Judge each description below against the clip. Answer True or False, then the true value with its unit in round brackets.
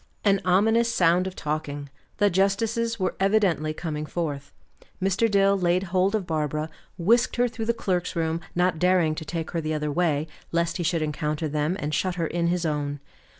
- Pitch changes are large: False (4.0 semitones)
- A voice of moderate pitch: True (175 Hz)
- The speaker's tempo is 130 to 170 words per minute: False (190 wpm)